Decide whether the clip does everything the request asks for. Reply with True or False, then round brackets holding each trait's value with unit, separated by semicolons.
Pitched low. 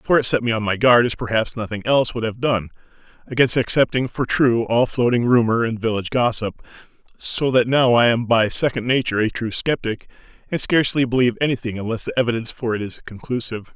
True (120 Hz)